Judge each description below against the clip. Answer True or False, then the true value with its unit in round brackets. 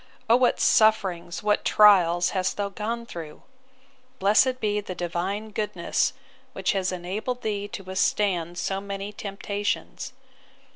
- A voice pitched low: False (200 Hz)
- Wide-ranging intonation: False (2.5 semitones)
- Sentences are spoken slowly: True (130 wpm)